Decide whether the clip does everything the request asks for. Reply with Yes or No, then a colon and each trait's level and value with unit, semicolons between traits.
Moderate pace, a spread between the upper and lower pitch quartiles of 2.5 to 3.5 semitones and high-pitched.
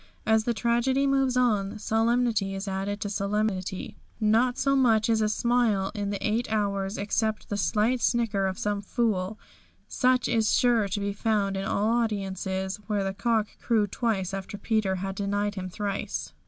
Yes: average, 175 wpm; average, 2.8 semitones; high, 210 Hz